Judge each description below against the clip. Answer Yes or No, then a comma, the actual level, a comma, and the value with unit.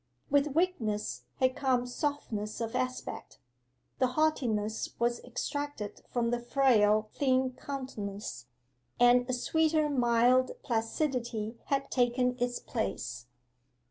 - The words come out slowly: Yes, slow, 110 wpm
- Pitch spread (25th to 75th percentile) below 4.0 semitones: Yes, average, 3.3 semitones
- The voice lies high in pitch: Yes, high, 245 Hz